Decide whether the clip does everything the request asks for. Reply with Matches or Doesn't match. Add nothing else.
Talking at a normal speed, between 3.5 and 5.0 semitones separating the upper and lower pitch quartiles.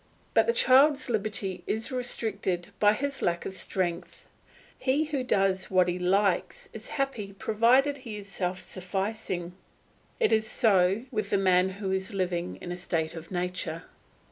Matches